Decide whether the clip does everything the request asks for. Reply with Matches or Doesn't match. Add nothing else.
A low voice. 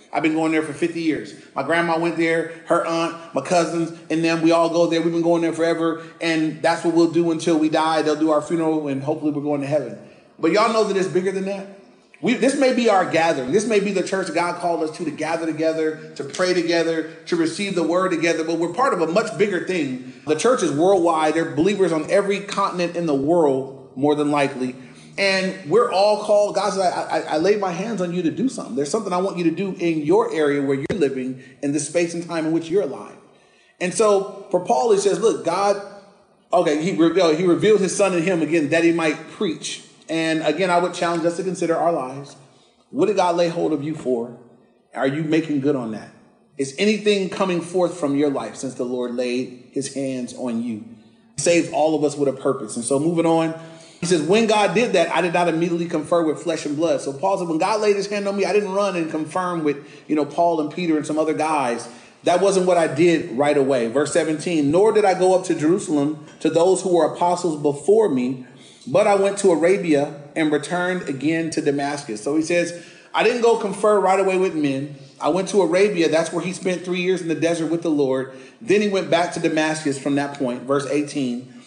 Doesn't match